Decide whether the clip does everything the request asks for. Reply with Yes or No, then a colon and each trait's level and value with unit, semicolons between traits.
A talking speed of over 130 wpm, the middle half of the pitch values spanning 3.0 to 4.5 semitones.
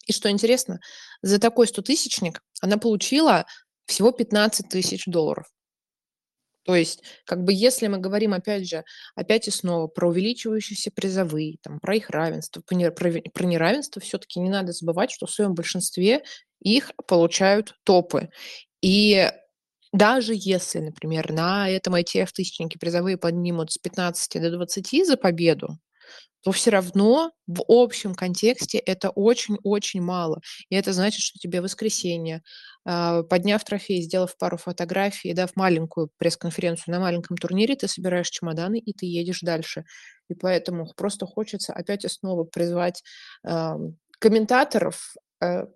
Yes: average, 140 wpm; average, 3.3 semitones